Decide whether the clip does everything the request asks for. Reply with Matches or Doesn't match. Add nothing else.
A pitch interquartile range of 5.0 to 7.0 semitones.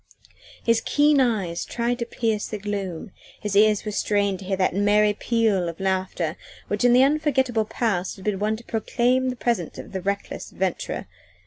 Doesn't match